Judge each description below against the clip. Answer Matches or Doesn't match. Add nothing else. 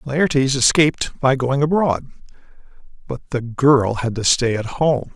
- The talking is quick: Doesn't match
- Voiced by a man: Matches